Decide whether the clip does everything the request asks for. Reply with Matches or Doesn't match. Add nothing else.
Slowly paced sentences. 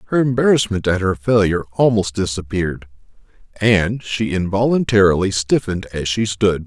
Matches